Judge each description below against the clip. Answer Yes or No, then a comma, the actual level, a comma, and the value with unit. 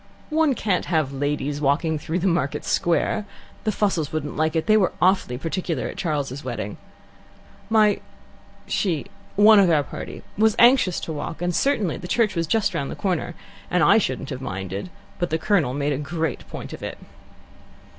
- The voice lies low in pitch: No, medium, 165 Hz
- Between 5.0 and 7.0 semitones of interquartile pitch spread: Yes, wide, 5.5 semitones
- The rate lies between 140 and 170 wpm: No, average, 180 wpm